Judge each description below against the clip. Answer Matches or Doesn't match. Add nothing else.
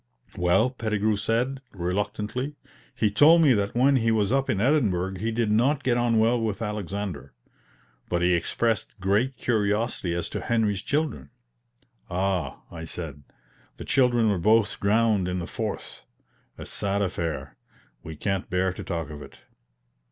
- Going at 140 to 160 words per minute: Matches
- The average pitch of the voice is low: Matches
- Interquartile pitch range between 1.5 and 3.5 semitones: Doesn't match